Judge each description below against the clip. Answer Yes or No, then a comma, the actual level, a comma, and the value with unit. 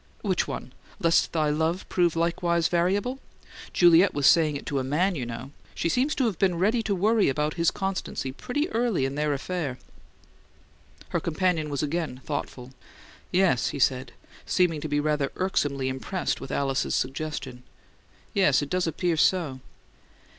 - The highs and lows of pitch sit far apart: No, average, 4.6 semitones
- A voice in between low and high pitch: Yes, medium, 160 Hz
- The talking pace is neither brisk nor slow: Yes, average, 160 wpm